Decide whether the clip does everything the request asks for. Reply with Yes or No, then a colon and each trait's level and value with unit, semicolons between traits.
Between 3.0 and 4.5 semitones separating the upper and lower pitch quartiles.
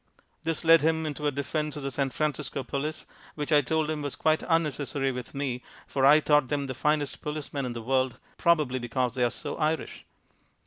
No: narrow, 2.6 semitones